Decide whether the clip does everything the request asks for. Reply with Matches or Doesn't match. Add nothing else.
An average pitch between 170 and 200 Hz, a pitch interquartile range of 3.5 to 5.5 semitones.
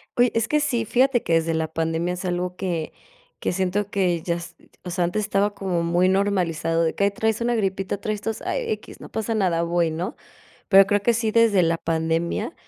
Matches